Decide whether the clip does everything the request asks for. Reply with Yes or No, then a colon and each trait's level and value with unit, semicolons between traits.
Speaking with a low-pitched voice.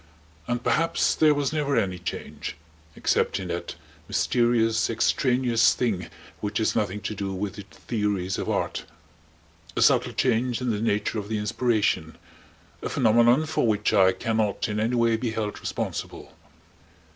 Yes: low, 110 Hz